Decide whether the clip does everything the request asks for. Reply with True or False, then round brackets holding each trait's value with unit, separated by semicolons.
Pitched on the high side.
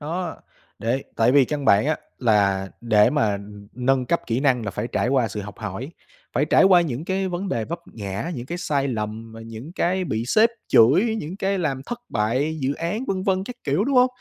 False (135 Hz)